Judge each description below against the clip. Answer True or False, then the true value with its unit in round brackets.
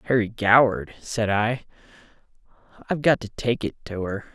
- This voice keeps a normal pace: True (150 wpm)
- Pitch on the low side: True (115 Hz)